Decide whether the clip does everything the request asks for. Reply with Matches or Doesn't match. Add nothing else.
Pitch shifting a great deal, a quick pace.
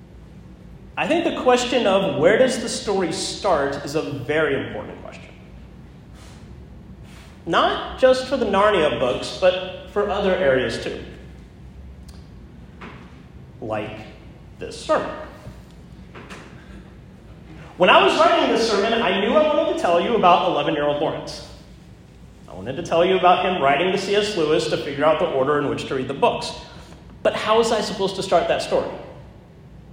Doesn't match